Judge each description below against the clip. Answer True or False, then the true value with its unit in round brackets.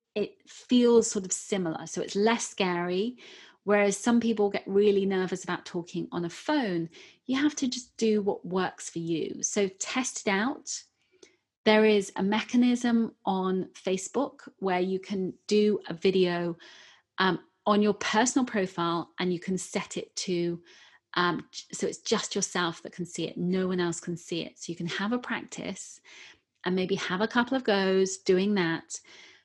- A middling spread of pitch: True (4.0 semitones)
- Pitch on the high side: True (200 Hz)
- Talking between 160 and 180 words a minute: True (175 wpm)